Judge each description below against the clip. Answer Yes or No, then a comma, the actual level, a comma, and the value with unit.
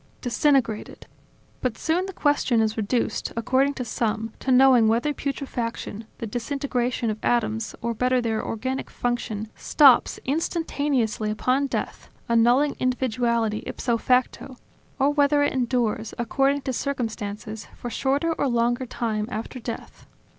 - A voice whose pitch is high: Yes, high, 245 Hz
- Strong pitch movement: No, average, 3.2 semitones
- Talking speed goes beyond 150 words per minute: No, slow, 135 wpm